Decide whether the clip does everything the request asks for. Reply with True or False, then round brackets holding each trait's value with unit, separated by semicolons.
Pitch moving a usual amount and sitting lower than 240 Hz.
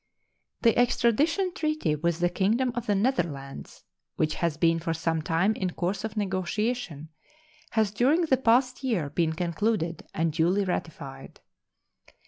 False (6.3 semitones; 190 Hz)